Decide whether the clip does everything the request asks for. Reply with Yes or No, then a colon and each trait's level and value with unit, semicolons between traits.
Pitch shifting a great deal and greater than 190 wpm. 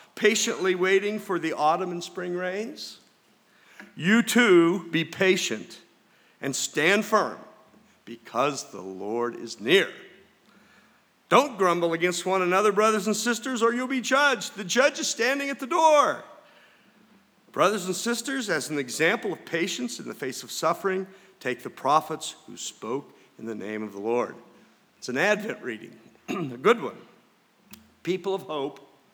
No: wide, 5.8 semitones; average, 150 wpm